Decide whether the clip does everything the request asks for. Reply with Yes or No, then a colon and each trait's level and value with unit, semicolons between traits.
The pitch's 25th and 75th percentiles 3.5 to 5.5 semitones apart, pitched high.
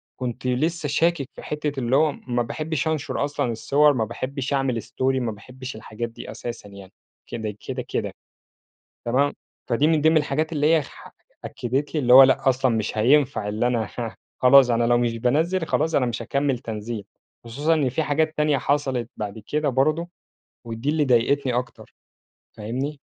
No: average, 4.0 semitones; low, 130 Hz